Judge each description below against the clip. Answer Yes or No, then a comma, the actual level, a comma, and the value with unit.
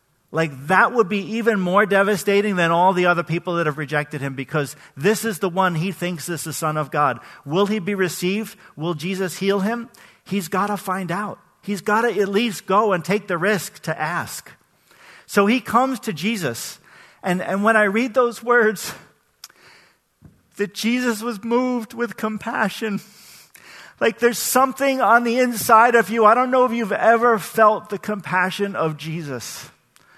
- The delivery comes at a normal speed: Yes, average, 180 wpm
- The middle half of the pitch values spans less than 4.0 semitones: No, average, 4.5 semitones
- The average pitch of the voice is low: No, high, 200 Hz